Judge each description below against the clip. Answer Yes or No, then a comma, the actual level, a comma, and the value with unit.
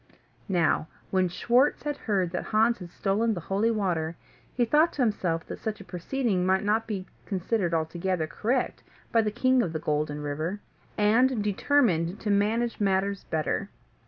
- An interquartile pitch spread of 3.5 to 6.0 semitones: Yes, average, 4.7 semitones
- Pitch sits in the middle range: No, high, 200 Hz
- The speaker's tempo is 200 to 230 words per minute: No, average, 165 wpm